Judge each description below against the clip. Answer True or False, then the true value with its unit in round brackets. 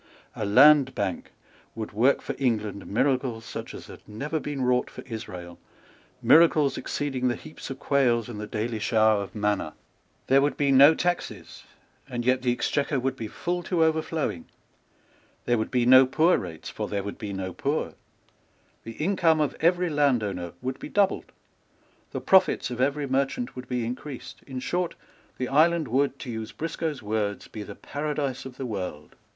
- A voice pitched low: True (130 Hz)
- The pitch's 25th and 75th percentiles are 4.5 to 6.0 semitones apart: True (5.0 semitones)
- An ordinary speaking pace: True (175 wpm)